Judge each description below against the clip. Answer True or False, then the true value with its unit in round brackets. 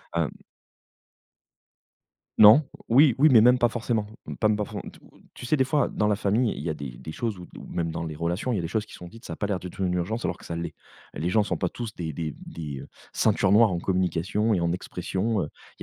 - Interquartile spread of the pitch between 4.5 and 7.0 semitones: True (4.9 semitones)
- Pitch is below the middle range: True (100 Hz)